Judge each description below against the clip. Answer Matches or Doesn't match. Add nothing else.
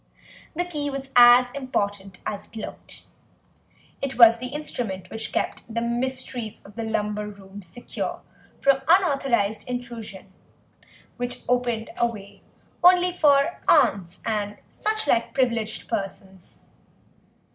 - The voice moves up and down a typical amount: Matches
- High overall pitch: Matches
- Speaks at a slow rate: Matches